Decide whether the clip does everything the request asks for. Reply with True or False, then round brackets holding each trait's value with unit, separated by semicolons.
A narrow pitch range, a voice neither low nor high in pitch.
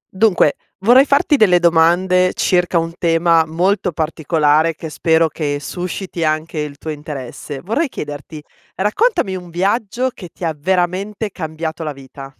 False (3.4 semitones; 170 Hz)